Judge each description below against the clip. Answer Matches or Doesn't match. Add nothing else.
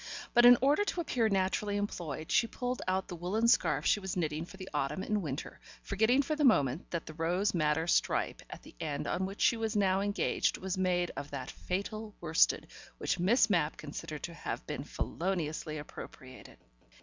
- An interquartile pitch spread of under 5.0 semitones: Doesn't match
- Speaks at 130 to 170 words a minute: Doesn't match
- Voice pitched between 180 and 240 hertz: Matches